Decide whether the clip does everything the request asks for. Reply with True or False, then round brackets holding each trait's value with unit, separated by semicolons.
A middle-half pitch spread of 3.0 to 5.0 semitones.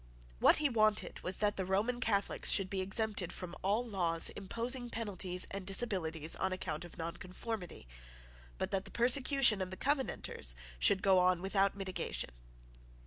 True (3.6 semitones)